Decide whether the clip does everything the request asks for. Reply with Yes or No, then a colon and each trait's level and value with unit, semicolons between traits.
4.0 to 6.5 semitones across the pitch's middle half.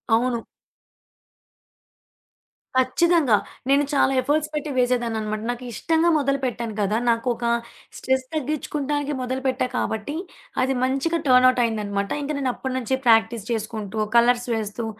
No: average, 3.5 semitones